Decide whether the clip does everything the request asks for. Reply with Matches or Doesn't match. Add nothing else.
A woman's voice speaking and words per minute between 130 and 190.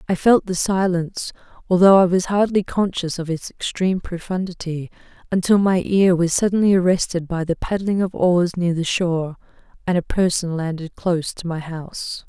Matches